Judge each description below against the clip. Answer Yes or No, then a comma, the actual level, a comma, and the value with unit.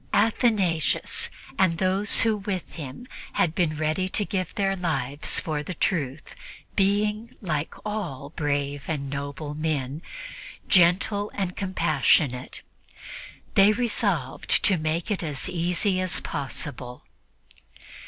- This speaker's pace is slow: Yes, slow, 115 wpm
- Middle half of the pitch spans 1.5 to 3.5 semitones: No, average, 5.2 semitones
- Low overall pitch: No, medium, 170 Hz